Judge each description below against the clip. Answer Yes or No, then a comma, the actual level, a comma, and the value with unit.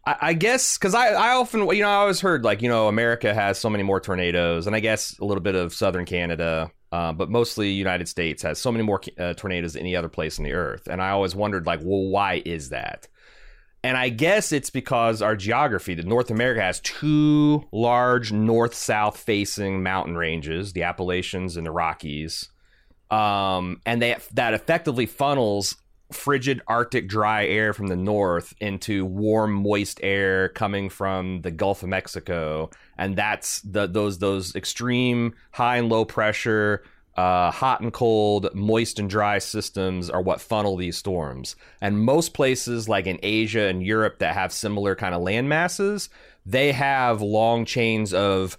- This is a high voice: No, low, 105 Hz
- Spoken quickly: No, average, 180 wpm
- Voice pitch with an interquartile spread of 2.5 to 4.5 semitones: Yes, average, 4.1 semitones